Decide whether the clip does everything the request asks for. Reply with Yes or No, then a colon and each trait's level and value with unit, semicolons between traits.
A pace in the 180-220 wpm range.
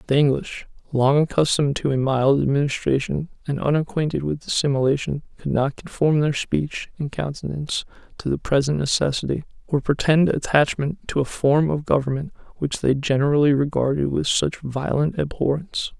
No: average, 145 wpm